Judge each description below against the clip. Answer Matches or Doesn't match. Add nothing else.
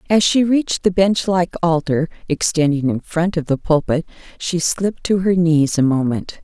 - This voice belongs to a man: Doesn't match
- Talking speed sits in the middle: Matches